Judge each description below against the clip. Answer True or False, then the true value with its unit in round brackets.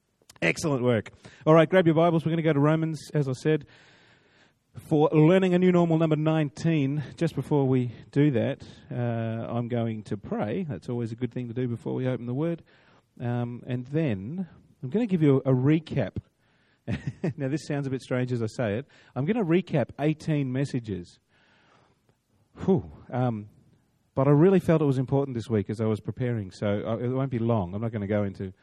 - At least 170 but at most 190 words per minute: False (205 wpm)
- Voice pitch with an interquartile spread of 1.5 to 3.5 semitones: False (4.8 semitones)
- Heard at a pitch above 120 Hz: True (135 Hz)